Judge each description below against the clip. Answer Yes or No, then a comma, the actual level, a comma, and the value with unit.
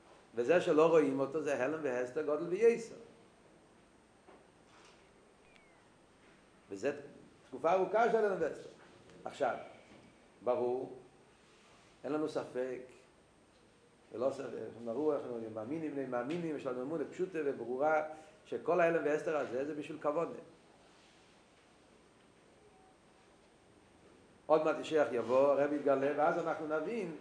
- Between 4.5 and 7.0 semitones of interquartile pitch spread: No, average, 3.0 semitones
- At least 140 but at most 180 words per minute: No, average, 115 wpm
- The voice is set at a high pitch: No, medium, 155 Hz